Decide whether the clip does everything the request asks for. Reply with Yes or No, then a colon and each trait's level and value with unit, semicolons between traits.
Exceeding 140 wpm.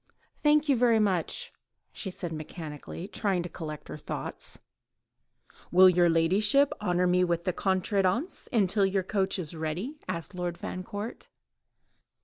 No: slow, 135 wpm